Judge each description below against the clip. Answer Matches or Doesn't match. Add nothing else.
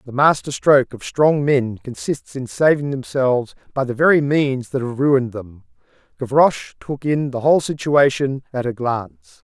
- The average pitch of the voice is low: Matches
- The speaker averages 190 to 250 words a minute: Doesn't match